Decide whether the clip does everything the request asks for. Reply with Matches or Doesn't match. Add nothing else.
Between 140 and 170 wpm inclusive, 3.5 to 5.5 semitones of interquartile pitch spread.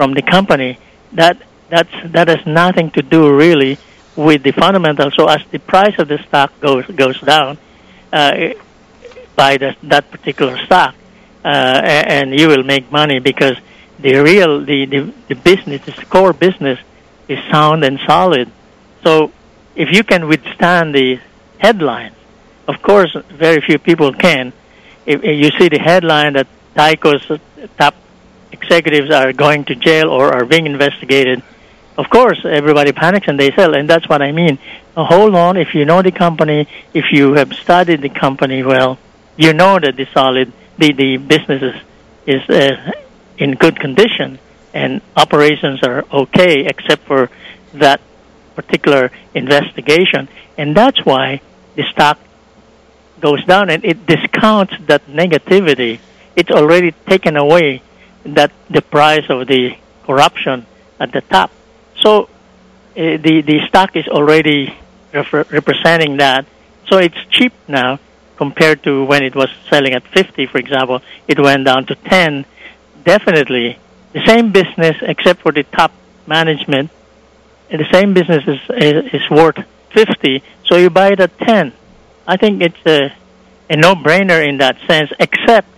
Matches